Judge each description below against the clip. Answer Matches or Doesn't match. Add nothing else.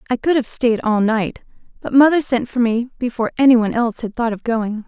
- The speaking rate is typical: Doesn't match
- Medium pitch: Doesn't match